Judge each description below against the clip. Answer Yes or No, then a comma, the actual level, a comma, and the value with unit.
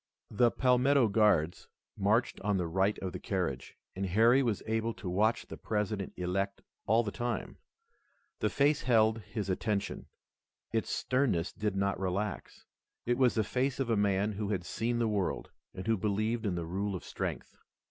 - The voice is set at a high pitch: No, low, 105 Hz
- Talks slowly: No, average, 175 wpm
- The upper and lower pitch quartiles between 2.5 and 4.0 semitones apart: Yes, average, 3.1 semitones